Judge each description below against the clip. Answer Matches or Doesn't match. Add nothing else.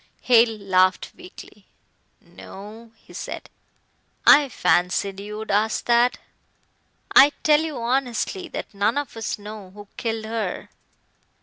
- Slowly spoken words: Matches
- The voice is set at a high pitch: Matches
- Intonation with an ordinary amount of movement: Matches